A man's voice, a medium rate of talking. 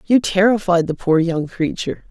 No: female; average, 170 wpm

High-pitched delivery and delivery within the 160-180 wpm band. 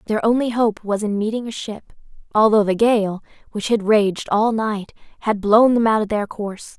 No: high, 215 Hz; fast, 205 wpm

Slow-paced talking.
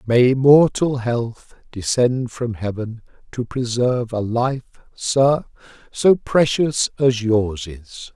Yes: slow, 120 wpm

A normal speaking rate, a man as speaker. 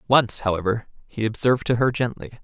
Yes: average, 175 wpm; male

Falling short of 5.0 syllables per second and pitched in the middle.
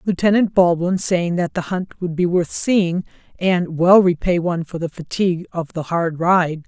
Yes: 4.6 syllables/s; medium, 175 Hz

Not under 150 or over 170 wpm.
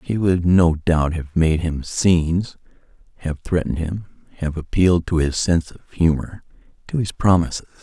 Yes: average, 160 wpm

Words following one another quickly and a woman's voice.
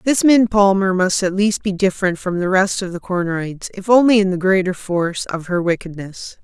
Yes: fast, 215 wpm; female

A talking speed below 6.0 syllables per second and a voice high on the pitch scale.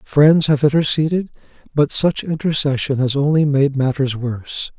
No: 4.8 syllables/s; medium, 145 Hz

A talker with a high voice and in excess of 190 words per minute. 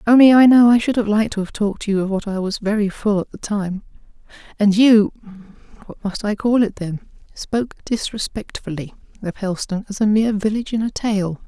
Yes: high, 210 Hz; average, 200 wpm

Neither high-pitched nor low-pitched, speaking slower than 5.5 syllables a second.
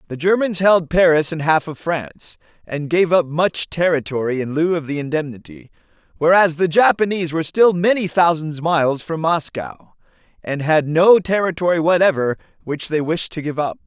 Yes: medium, 165 Hz; 5.1 syllables/s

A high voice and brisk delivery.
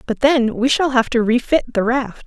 Yes: high, 245 Hz; fast, 240 wpm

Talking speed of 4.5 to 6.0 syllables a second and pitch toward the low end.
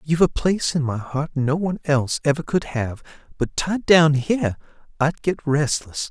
No: 5.0 syllables/s; medium, 150 Hz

